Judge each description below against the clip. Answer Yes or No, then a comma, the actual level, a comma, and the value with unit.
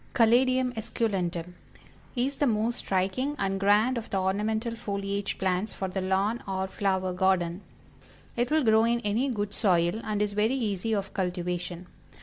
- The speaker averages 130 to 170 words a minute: Yes, average, 155 wpm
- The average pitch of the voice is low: No, high, 205 Hz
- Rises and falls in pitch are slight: No, average, 3.4 semitones